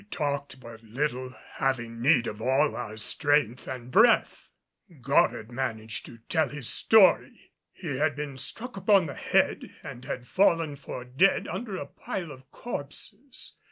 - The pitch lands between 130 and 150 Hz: Yes, medium, 140 Hz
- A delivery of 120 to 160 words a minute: Yes, average, 155 wpm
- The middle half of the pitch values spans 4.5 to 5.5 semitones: Yes, average, 5.0 semitones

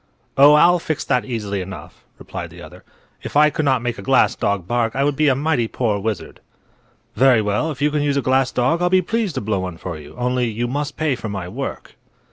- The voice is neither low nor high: No, low, 125 Hz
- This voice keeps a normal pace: No, fast, 240 wpm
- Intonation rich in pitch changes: Yes, wide, 5.7 semitones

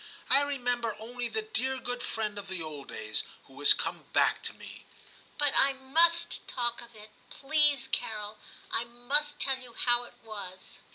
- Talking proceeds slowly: No, average, 185 wpm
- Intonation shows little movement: No, average, 4.3 semitones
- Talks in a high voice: Yes, high, 245 Hz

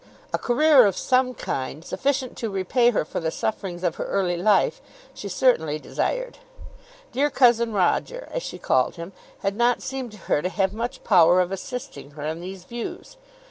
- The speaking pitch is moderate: No, high, 205 Hz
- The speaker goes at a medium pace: Yes, average, 180 wpm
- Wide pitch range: Yes, wide, 6.0 semitones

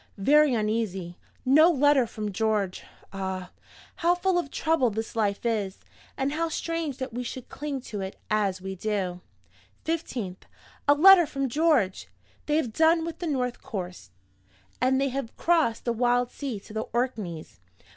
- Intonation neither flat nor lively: No, wide, 6.4 semitones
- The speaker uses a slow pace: No, average, 160 wpm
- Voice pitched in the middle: No, high, 245 Hz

